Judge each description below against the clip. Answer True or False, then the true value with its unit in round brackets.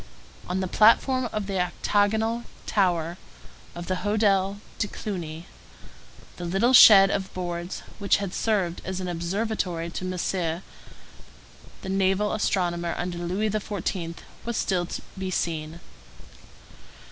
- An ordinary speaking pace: False (125 wpm)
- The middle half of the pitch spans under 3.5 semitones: True (3.0 semitones)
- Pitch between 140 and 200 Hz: True (190 Hz)